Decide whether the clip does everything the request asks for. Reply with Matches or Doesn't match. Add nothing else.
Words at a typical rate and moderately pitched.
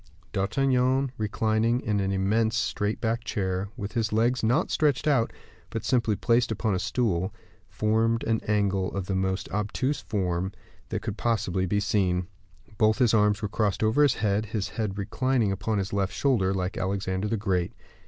Doesn't match